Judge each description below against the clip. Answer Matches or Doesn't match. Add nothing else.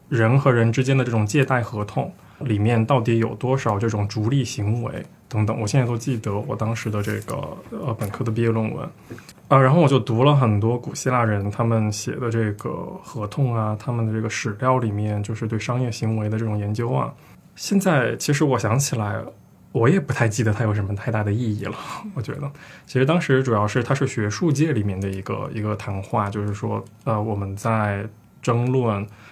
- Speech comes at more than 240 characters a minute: Matches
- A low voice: Matches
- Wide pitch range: Doesn't match